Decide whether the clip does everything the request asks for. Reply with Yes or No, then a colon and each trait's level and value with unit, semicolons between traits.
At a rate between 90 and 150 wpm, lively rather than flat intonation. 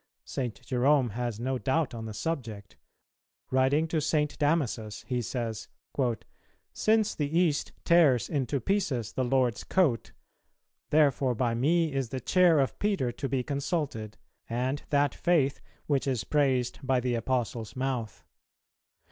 No: average, 140 wpm; average, 3.7 semitones